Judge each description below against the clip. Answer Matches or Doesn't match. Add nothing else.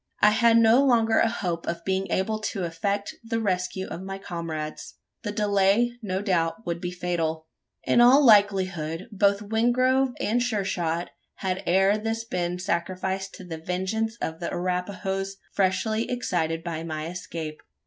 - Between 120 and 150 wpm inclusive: Doesn't match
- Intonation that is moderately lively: Matches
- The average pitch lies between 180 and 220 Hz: Matches